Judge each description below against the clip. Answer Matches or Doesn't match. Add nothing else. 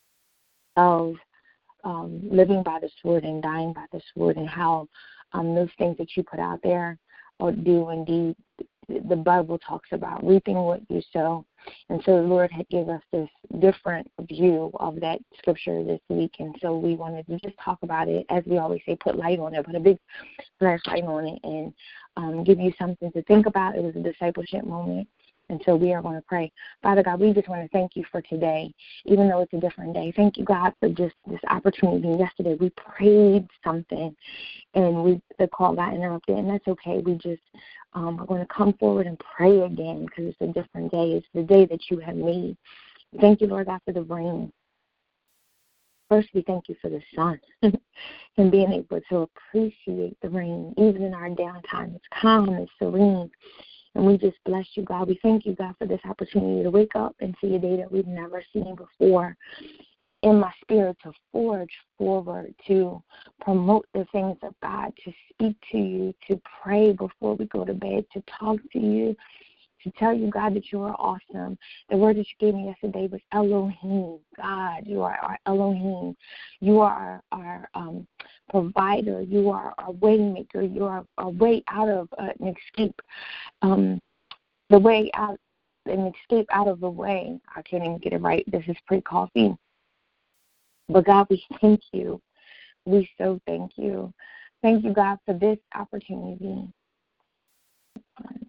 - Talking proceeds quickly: Doesn't match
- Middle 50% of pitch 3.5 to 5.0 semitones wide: Doesn't match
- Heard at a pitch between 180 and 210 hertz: Matches